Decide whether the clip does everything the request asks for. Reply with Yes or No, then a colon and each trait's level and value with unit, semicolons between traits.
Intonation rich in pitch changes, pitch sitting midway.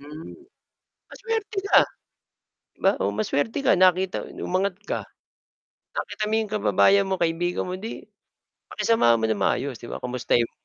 Yes: wide, 8.8 semitones; medium, 180 Hz